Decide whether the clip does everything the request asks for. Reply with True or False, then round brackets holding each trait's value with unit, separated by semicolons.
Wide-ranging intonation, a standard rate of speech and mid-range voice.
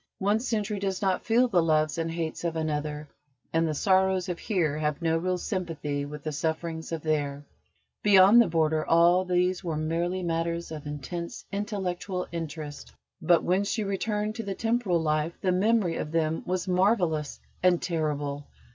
False (3.4 semitones; 170 wpm; 170 Hz)